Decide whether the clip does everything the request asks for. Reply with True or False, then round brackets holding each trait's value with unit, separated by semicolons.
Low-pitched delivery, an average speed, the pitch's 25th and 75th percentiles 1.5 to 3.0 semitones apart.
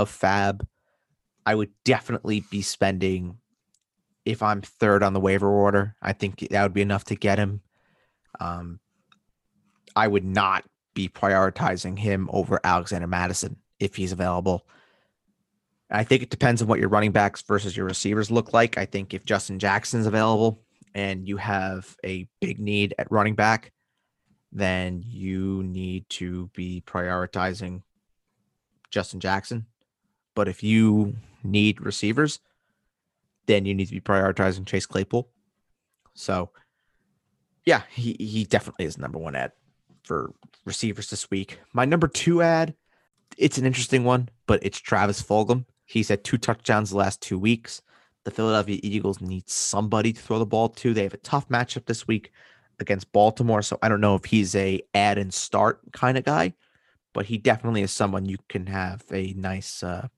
True (100 Hz; 160 wpm; 2.6 semitones)